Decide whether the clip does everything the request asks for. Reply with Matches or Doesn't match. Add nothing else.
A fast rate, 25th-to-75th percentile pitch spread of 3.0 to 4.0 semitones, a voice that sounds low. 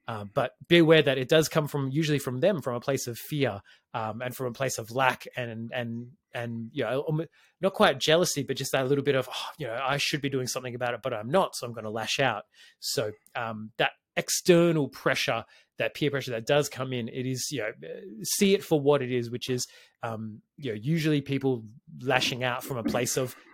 Matches